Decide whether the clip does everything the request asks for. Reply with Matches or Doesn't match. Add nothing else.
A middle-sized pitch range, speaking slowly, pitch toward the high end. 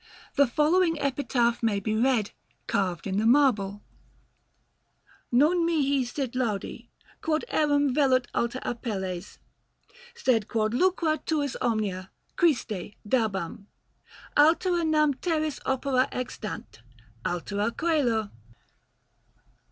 Doesn't match